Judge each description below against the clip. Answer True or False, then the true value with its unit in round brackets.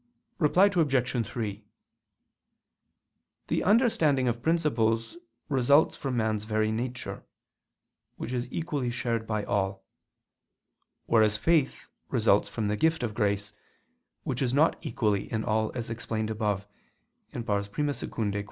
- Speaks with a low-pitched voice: True (115 Hz)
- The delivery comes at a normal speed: False (125 wpm)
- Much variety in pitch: False (4.5 semitones)